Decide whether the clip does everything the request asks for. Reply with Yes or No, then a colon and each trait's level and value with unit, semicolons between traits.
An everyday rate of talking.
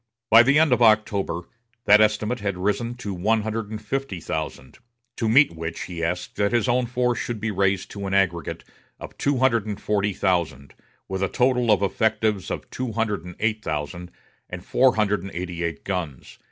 Yes: average, 195 wpm